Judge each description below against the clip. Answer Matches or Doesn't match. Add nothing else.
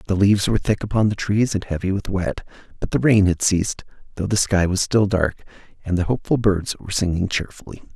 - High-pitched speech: Doesn't match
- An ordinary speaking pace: Doesn't match